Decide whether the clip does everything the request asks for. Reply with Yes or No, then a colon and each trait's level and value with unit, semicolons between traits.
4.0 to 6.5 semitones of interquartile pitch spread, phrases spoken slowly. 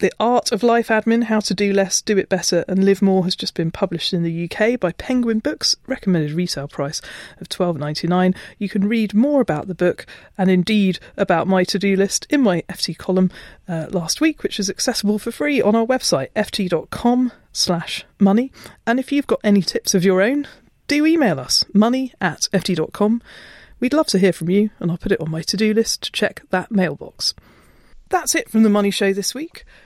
No: average, 4.3 semitones; fast, 205 wpm